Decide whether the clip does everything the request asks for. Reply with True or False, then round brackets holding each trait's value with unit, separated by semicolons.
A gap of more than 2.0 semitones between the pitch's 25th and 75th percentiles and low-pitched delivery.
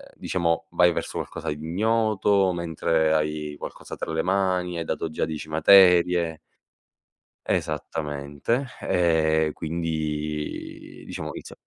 True (2.6 semitones; 80 Hz)